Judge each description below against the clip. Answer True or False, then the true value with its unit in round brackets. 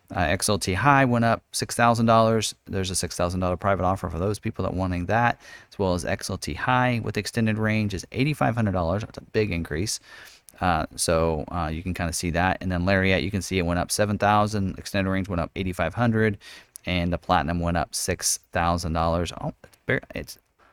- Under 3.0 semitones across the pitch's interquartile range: False (3.7 semitones)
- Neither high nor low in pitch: False (95 Hz)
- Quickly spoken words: True (225 wpm)